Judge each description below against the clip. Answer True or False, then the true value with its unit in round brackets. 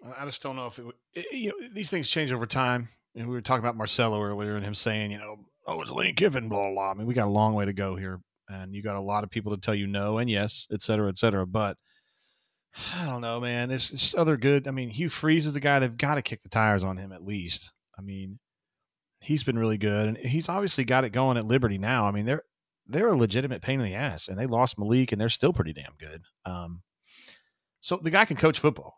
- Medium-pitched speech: False (115 Hz)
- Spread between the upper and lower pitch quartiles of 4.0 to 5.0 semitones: True (4.4 semitones)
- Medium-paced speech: False (270 wpm)